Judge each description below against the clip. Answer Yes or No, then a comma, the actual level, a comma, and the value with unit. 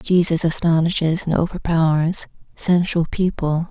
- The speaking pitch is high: No, medium, 165 Hz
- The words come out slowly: Yes, slow, 95 wpm